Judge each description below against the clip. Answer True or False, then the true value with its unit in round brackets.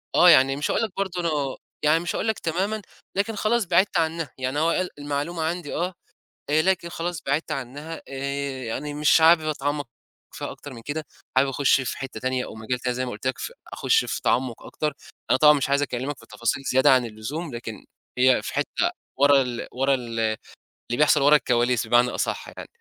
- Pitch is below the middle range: False (145 Hz)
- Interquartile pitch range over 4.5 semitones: False (4.2 semitones)